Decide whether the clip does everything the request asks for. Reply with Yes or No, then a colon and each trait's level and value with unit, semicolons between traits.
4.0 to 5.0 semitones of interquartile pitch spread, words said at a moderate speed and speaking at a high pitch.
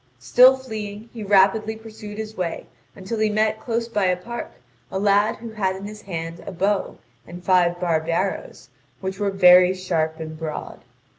No: average, 3.3 semitones; average, 175 wpm; high, 195 Hz